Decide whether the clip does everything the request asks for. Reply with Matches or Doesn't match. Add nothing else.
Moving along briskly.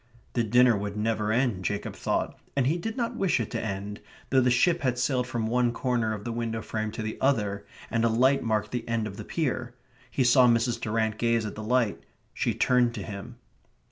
Matches